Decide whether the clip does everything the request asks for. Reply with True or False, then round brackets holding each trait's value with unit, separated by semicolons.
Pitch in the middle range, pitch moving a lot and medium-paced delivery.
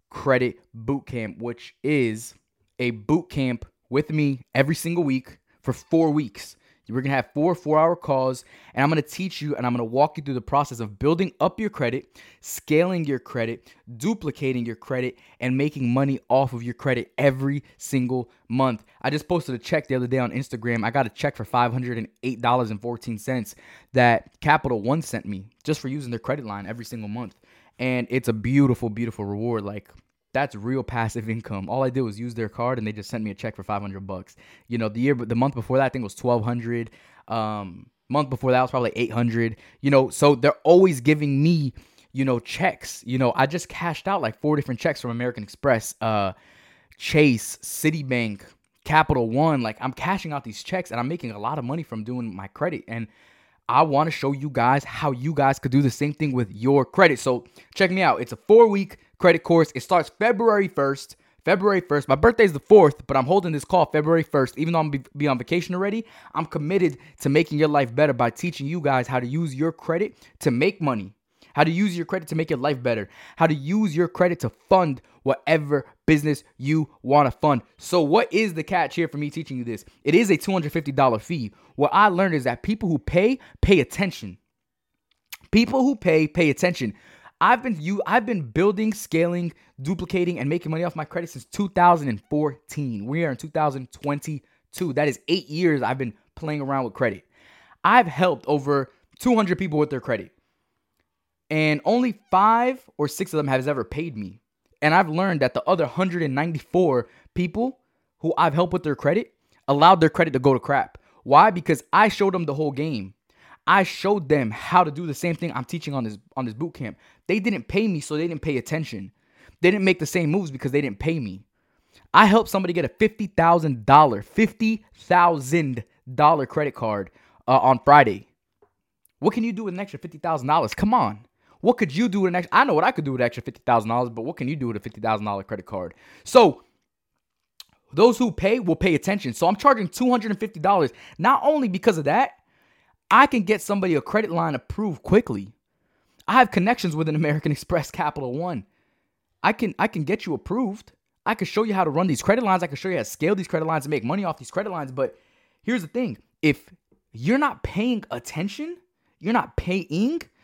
False (145 Hz; 6.1 semitones; 210 wpm)